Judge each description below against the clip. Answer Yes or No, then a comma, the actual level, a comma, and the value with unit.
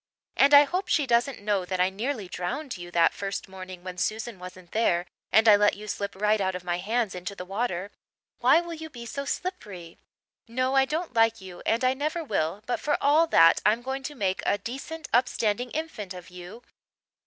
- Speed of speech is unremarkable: No, fast, 210 wpm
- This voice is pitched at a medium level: No, high, 215 Hz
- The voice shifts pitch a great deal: Yes, wide, 6.2 semitones